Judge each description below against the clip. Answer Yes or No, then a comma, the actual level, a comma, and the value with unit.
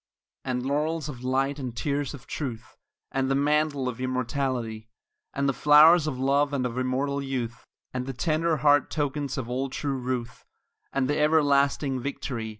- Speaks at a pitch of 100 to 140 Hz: Yes, low, 135 Hz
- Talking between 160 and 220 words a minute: Yes, average, 170 wpm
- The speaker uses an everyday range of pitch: No, narrow, 2.3 semitones